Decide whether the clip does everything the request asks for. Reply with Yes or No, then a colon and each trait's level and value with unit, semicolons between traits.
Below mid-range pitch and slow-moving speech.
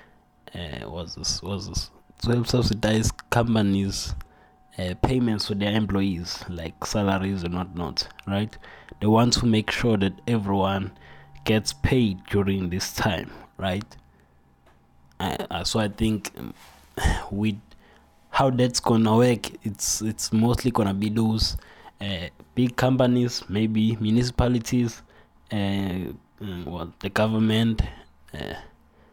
Yes: low, 100 Hz; slow, 120 wpm